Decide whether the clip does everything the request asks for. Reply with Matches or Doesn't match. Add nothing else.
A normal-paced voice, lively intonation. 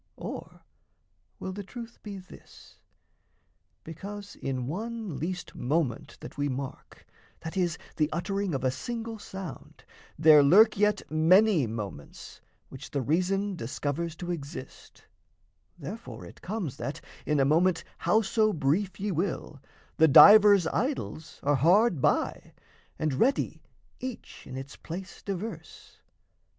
Doesn't match